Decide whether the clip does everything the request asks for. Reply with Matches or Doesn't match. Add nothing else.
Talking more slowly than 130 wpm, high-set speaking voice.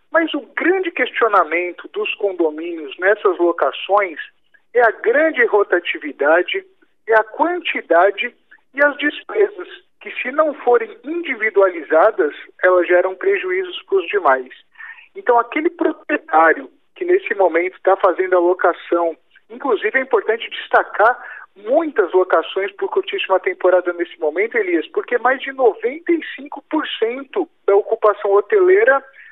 Matches